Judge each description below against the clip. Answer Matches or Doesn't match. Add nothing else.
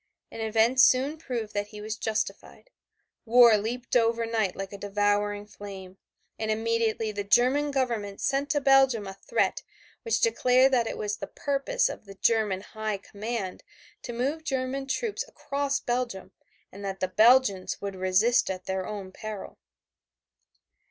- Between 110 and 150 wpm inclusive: Doesn't match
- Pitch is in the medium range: Doesn't match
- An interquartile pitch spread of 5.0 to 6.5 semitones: Doesn't match